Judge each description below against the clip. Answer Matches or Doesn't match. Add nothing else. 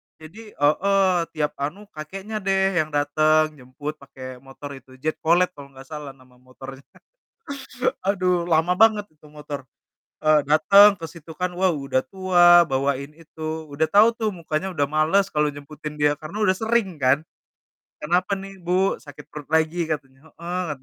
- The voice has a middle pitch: Matches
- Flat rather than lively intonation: Doesn't match